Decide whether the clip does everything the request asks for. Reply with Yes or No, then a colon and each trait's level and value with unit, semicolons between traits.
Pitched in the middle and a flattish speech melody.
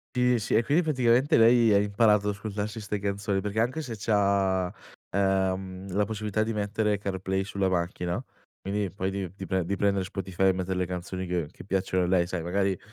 No: low, 100 Hz; narrow, 2.2 semitones